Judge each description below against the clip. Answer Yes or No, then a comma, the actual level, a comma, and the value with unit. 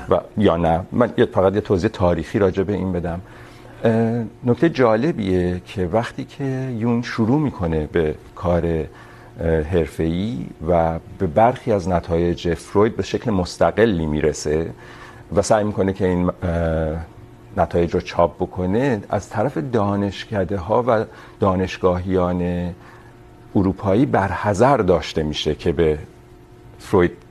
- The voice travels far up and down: No, average, 4.6 semitones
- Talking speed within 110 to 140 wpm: Yes, average, 120 wpm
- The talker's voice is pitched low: Yes, very low, 95 Hz